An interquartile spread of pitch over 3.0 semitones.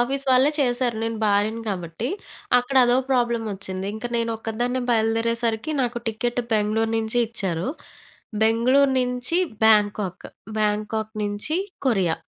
No: narrow, 2.6 semitones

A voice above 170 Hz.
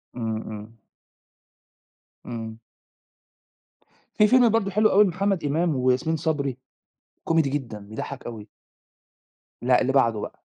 No: medium, 140 Hz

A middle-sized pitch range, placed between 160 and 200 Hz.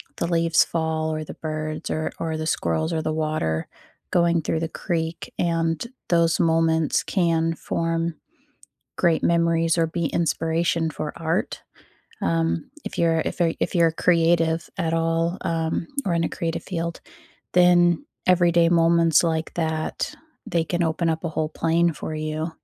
No: narrow, 1.0 semitones; medium, 165 Hz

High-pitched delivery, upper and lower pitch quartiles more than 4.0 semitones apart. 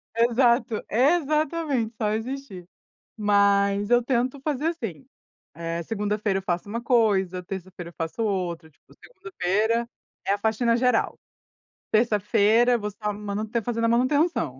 No: high, 220 Hz; average, 3.5 semitones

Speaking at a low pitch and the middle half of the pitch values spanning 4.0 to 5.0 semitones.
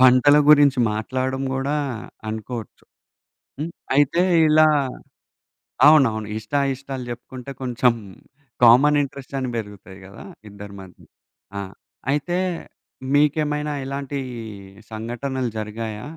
Yes: low, 130 Hz; average, 4.4 semitones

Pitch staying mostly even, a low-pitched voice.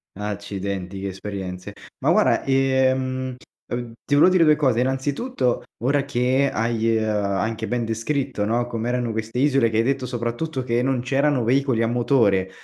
No: average, 3.2 semitones; low, 120 Hz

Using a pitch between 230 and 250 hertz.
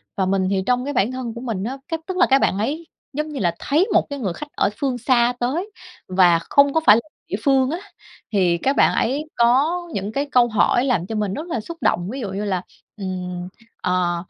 Yes: high, 240 Hz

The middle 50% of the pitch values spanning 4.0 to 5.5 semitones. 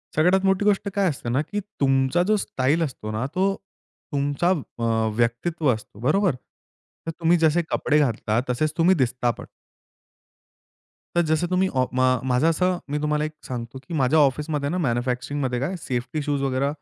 Yes: average, 5.1 semitones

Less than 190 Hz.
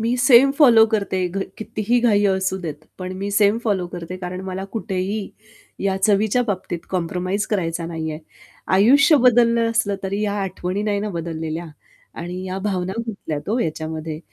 No: high, 195 Hz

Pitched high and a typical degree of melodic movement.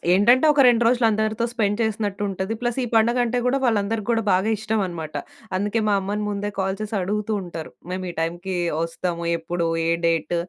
Yes: high, 205 Hz; average, 3.5 semitones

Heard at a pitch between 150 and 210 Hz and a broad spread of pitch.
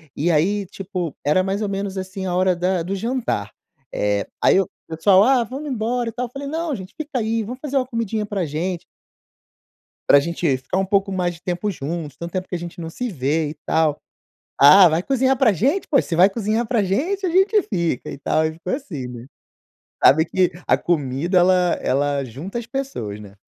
Yes: medium, 185 Hz; wide, 6.1 semitones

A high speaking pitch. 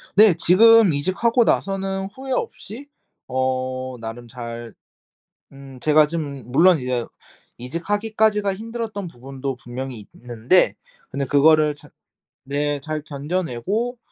No: medium, 150 Hz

